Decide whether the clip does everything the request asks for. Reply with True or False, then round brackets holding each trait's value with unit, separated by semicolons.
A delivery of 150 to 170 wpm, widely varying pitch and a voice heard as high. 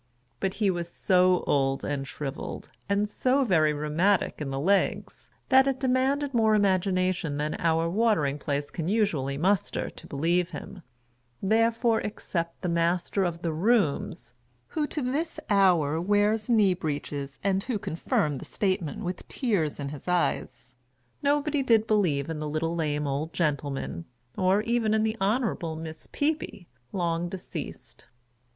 False (155 wpm; 5.9 semitones; 180 Hz)